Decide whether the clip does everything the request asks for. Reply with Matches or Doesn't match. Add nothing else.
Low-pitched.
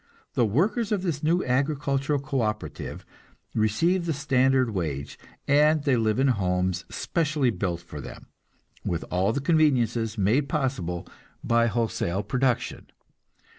Matches